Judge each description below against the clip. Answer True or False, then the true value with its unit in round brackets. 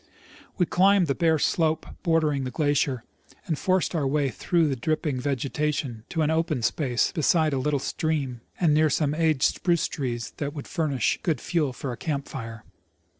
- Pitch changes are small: False (3.2 semitones)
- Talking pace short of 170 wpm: False (175 wpm)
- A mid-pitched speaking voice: True (150 Hz)